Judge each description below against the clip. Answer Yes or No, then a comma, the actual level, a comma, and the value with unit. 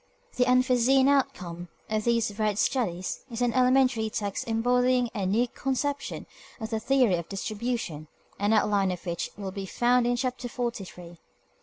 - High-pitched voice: Yes, high, 230 Hz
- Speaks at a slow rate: No, average, 160 wpm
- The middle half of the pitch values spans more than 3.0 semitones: Yes, average, 4.0 semitones